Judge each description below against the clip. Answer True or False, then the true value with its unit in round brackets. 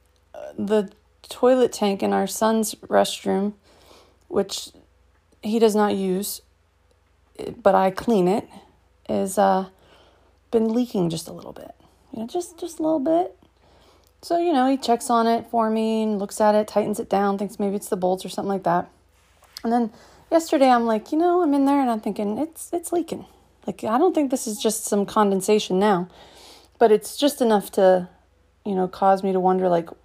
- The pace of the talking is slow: False (190 wpm)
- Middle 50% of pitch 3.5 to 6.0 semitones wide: True (4.0 semitones)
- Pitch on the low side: False (210 Hz)